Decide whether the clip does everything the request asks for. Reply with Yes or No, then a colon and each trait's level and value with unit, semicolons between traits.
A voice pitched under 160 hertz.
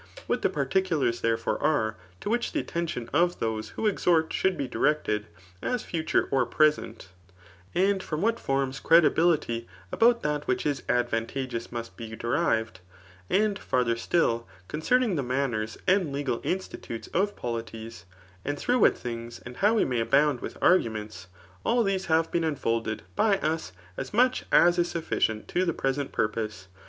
Yes: medium, 140 Hz